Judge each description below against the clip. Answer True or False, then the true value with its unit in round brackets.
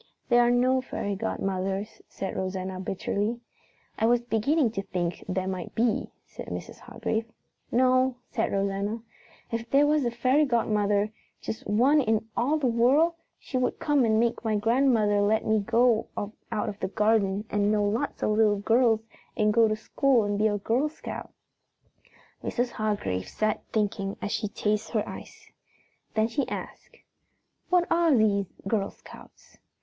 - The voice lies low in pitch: False (220 Hz)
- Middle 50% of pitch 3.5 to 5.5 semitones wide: False (3.0 semitones)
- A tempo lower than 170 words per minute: True (160 wpm)